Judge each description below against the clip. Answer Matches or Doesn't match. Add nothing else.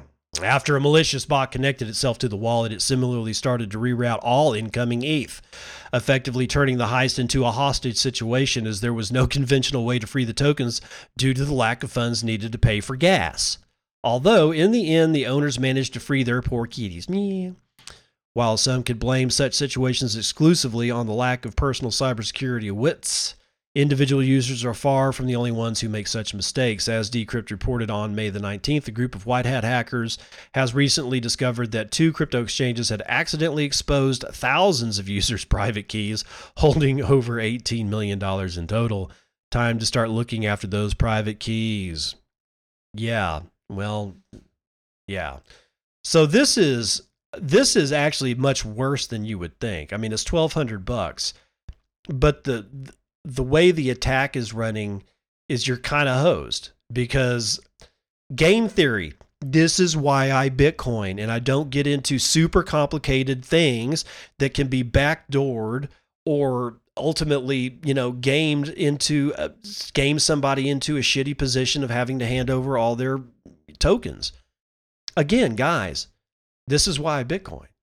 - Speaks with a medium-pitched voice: Doesn't match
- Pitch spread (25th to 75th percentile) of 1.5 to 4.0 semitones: Matches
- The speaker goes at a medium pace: Matches